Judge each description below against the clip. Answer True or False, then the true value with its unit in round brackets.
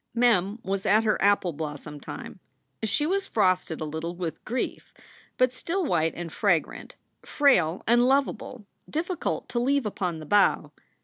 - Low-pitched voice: False (205 Hz)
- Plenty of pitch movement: True (7.0 semitones)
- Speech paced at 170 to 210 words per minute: False (160 wpm)